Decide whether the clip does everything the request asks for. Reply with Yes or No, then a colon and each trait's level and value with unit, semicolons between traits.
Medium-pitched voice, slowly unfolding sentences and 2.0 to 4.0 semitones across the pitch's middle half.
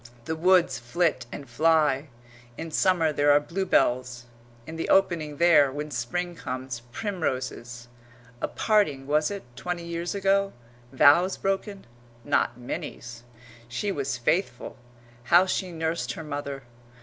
No: medium, 155 Hz; slow, 130 wpm; average, 5.1 semitones